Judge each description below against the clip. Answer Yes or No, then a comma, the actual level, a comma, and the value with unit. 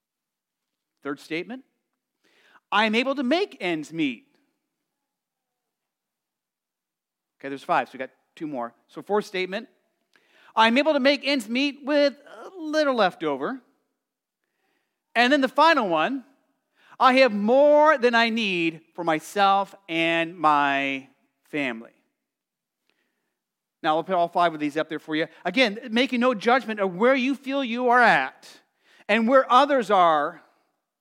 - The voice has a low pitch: No, high, 245 Hz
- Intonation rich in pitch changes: Yes, wide, 8.6 semitones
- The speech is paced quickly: No, average, 140 wpm